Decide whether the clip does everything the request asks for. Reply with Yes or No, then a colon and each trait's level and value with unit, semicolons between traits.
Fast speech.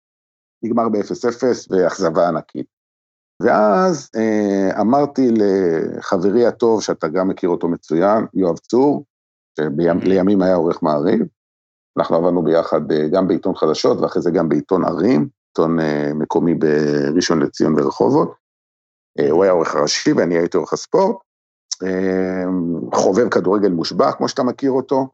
No: average, 125 wpm